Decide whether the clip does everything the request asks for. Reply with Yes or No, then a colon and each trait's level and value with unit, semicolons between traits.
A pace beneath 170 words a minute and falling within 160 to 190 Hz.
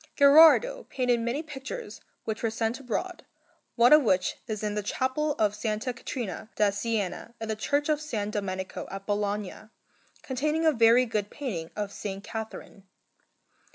No: average, 155 wpm; high, 225 Hz